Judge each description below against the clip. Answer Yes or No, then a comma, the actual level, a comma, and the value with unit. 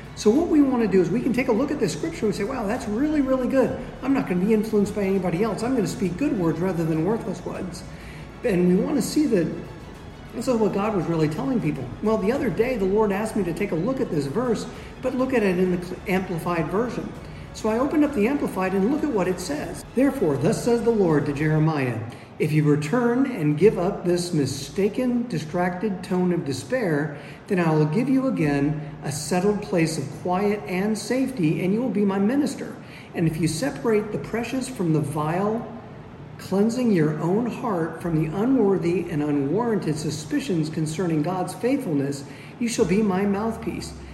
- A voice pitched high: Yes, high, 195 Hz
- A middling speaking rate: No, fast, 210 wpm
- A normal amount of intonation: No, wide, 6.3 semitones